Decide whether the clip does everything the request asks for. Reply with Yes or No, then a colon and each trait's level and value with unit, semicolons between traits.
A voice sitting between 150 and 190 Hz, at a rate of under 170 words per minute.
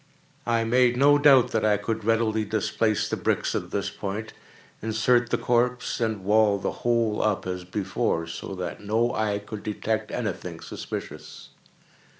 No: low, 110 Hz; average, 160 wpm